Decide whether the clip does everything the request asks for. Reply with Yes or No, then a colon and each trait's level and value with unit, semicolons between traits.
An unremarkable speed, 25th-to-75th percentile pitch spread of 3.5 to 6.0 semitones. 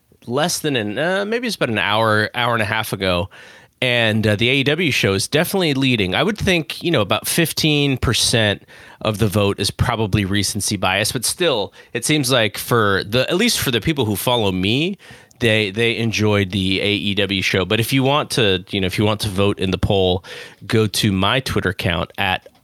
No: fast, 210 wpm; average, 4.4 semitones